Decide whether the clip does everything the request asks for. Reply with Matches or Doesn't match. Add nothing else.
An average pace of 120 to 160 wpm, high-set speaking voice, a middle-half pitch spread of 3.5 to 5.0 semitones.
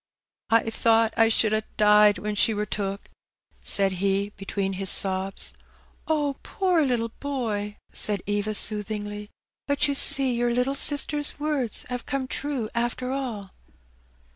Matches